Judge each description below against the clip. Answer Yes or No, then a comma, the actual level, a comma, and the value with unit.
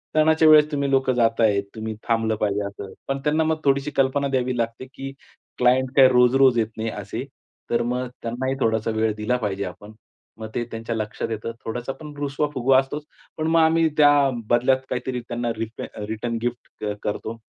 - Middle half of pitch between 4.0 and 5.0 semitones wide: No, average, 3.4 semitones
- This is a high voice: No, low, 125 Hz